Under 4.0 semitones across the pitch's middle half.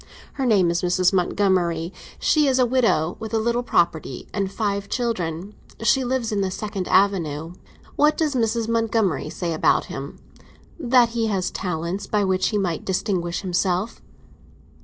No: average, 4.5 semitones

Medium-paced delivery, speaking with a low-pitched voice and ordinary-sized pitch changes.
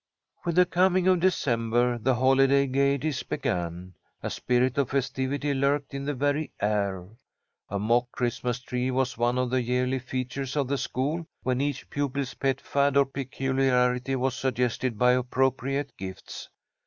No: average, 155 wpm; low, 130 Hz; narrow, 2.1 semitones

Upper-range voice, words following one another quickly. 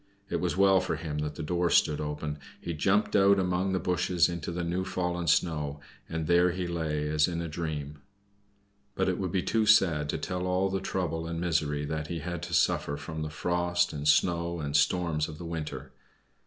No: very low, 85 Hz; fast, 210 wpm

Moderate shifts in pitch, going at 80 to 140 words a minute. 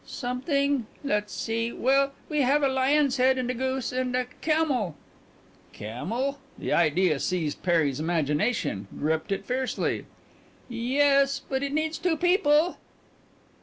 No: wide, 6.1 semitones; slow, 135 wpm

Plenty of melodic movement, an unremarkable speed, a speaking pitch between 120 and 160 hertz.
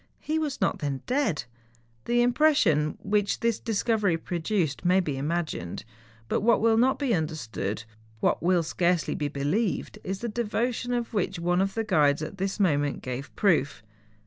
No: wide, 7.1 semitones; average, 170 wpm; medium, 185 Hz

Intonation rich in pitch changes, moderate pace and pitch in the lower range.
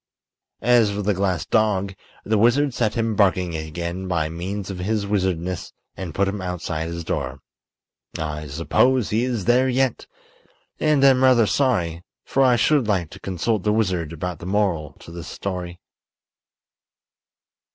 No: average, 4.8 semitones; average, 155 wpm; very low, 95 Hz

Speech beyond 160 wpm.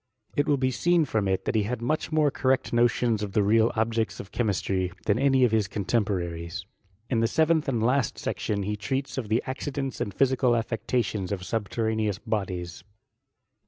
Yes: average, 180 wpm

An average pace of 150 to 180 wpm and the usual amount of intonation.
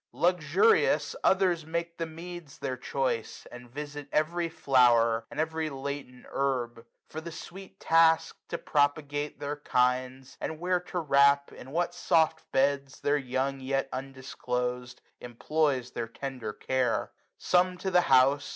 No: average, 140 wpm; average, 3.9 semitones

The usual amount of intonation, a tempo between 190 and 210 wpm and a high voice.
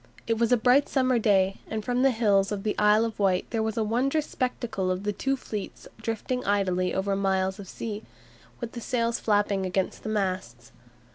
Yes: average, 3.3 semitones; average, 200 wpm; high, 215 Hz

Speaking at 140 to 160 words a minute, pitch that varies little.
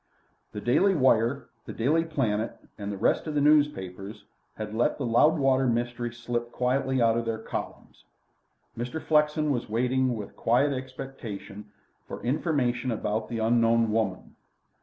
No: average, 145 wpm; average, 3.2 semitones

